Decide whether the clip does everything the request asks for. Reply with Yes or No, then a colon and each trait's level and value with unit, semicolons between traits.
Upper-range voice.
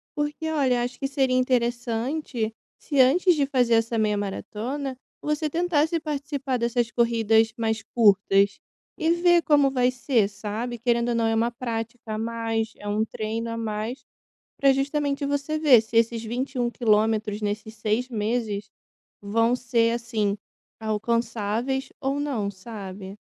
Yes: high, 235 Hz